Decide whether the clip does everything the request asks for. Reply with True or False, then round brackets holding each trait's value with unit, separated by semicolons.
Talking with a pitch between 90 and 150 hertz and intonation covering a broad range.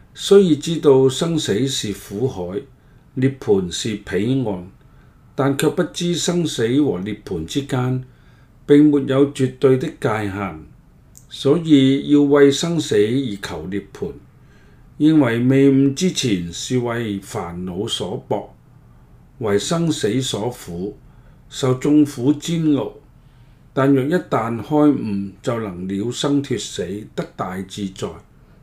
False (135 Hz; 4.2 semitones)